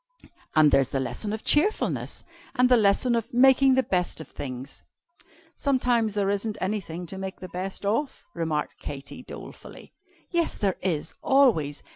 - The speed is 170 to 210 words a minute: No, average, 155 wpm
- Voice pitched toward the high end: Yes, high, 200 Hz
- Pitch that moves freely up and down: Yes, wide, 7.6 semitones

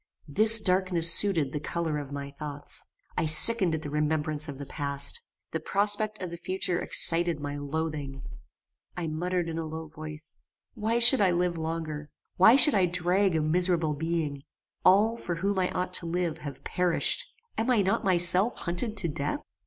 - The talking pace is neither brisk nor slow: Yes, average, 175 wpm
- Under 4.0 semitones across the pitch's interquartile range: Yes, average, 3.6 semitones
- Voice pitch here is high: No, medium, 170 Hz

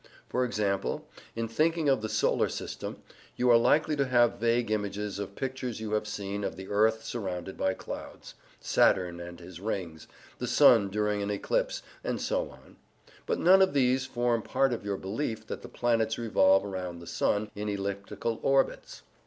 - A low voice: Yes, low, 110 Hz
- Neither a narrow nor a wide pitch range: Yes, average, 3.7 semitones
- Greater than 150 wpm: Yes, average, 180 wpm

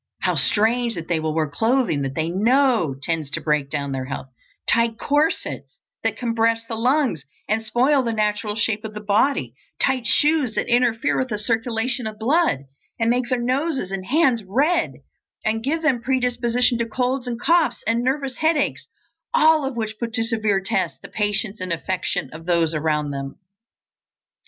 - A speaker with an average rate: Yes, average, 175 wpm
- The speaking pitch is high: Yes, high, 230 Hz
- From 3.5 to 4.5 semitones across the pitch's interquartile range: No, average, 4.9 semitones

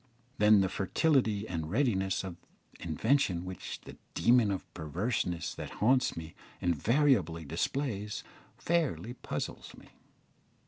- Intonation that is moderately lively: No, wide, 6.2 semitones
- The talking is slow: Yes, slow, 110 wpm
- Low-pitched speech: Yes, low, 100 Hz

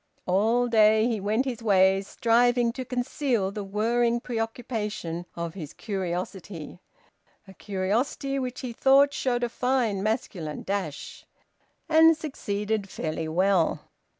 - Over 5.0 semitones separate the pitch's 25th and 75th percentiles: No, average, 4.2 semitones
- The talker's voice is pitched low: No, high, 220 Hz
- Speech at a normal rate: No, slow, 125 wpm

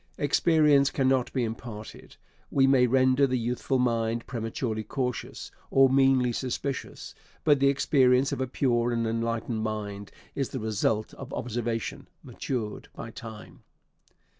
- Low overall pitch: Yes, low, 125 Hz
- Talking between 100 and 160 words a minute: Yes, slow, 135 wpm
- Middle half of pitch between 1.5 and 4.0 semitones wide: Yes, average, 2.9 semitones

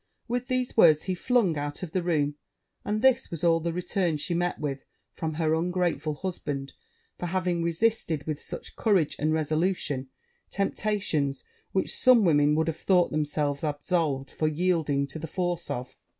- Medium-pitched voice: Yes, medium, 165 Hz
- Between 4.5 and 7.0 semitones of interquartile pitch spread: No, average, 3.7 semitones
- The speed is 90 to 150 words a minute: No, average, 165 wpm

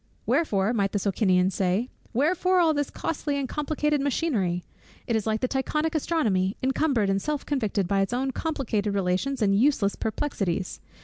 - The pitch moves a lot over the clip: Yes, wide, 6.9 semitones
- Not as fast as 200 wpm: Yes, average, 165 wpm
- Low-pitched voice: No, high, 235 Hz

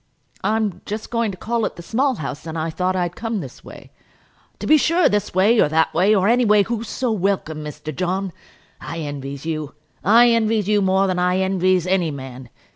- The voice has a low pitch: No, high, 190 Hz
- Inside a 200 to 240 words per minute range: Yes, fast, 205 wpm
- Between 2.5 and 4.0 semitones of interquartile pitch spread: No, average, 5.2 semitones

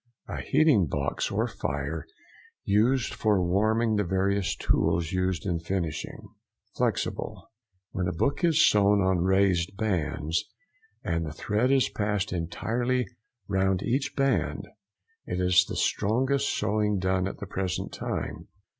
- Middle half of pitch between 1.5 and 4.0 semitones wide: Yes, average, 3.3 semitones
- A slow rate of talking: Yes, slow, 130 wpm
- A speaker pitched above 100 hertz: No, very low, 95 Hz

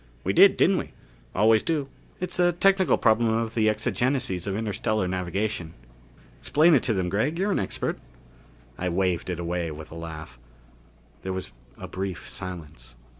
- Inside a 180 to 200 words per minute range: No, average, 165 wpm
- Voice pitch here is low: Yes, low, 100 Hz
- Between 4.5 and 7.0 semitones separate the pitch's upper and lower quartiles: Yes, average, 5.2 semitones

